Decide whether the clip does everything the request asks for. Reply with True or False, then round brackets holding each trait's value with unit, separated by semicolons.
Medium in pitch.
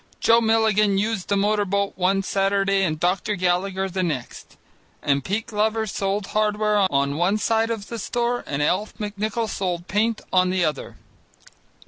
False (200 Hz)